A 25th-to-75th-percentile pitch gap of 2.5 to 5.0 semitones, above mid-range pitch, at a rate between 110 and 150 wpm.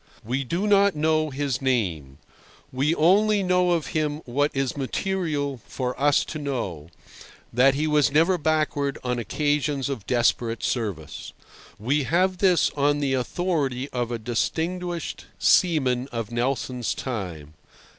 No: average, 4.3 semitones; medium, 140 Hz; slow, 135 wpm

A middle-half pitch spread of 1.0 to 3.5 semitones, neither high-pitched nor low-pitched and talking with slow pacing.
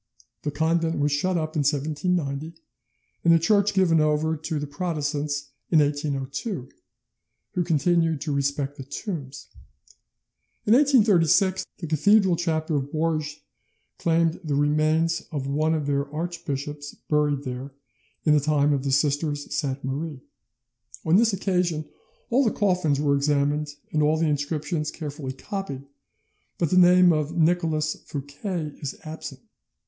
No: average, 2.7 semitones; medium, 155 Hz; average, 145 wpm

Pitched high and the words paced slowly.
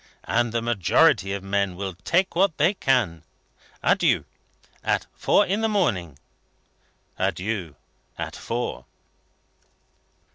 No: low, 110 Hz; slow, 115 wpm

